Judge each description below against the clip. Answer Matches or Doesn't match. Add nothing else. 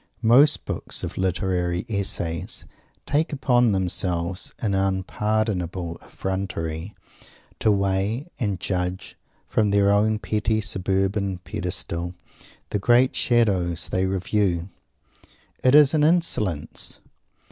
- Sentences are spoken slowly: Matches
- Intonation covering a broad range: Doesn't match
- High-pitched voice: Doesn't match